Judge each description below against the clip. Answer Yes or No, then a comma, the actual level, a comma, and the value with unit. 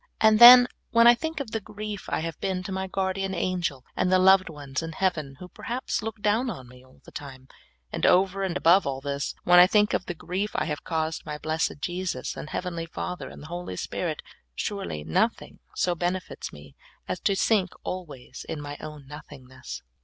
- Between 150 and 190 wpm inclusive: No, fast, 205 wpm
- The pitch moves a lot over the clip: No, average, 4.7 semitones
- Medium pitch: Yes, medium, 180 Hz